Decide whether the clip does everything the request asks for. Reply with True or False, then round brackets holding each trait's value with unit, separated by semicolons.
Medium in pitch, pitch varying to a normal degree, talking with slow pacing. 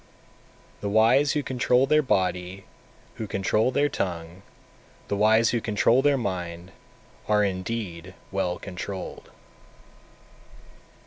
False (100 Hz; 4.9 semitones; 115 wpm)